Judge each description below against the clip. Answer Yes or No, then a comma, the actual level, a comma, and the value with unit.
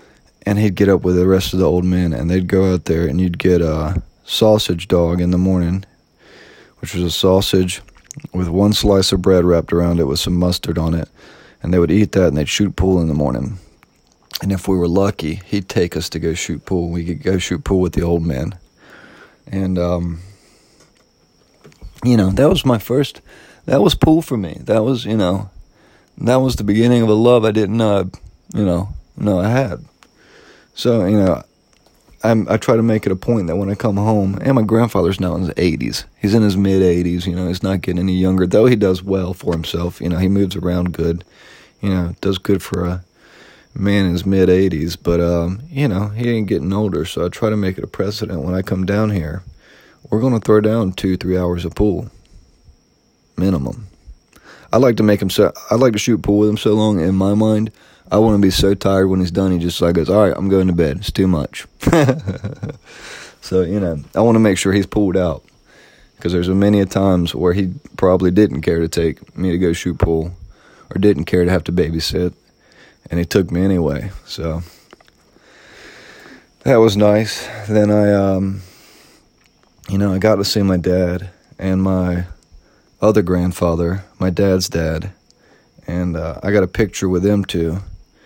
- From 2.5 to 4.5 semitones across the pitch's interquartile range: Yes, average, 2.8 semitones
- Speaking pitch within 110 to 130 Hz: No, very low, 95 Hz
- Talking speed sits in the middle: No, fast, 210 wpm